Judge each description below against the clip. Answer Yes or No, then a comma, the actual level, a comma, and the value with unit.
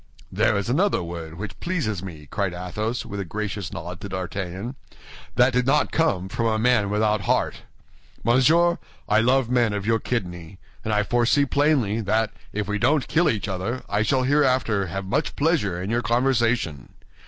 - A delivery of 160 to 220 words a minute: Yes, average, 180 wpm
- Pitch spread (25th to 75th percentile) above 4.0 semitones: Yes, average, 4.5 semitones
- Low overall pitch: Yes, low, 110 Hz